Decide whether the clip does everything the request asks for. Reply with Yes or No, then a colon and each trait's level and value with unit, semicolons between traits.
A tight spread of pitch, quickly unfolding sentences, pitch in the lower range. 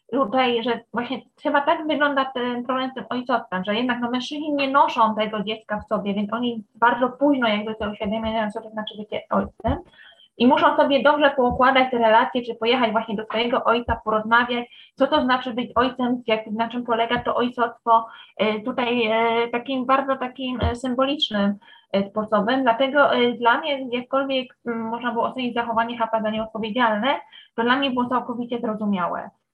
No: narrow, 2.3 semitones; fast, 175 wpm; high, 240 Hz